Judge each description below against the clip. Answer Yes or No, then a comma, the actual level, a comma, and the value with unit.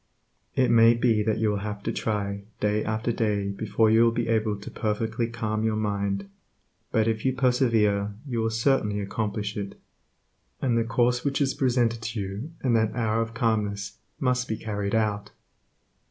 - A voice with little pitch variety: Yes, narrow, 2.1 semitones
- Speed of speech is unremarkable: Yes, average, 180 wpm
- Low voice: Yes, low, 110 Hz